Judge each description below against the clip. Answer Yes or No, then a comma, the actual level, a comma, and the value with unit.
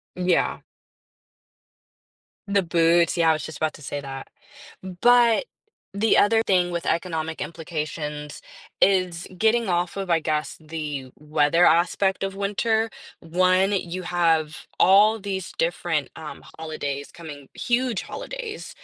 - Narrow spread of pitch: No, average, 4.0 semitones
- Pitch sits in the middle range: Yes, medium, 175 Hz